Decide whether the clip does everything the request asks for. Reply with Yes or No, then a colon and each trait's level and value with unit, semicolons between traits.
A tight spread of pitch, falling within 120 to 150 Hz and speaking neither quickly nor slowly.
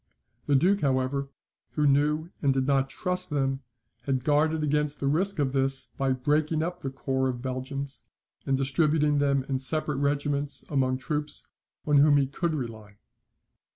Yes: narrow, 2.0 semitones; medium, 140 Hz; average, 160 wpm